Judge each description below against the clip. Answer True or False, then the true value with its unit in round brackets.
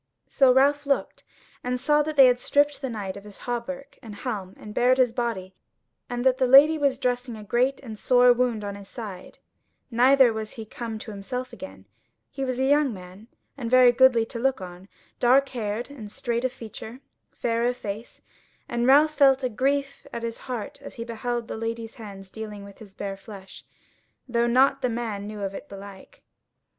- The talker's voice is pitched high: True (240 Hz)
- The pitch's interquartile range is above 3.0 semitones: True (3.6 semitones)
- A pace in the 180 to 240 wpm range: True (195 wpm)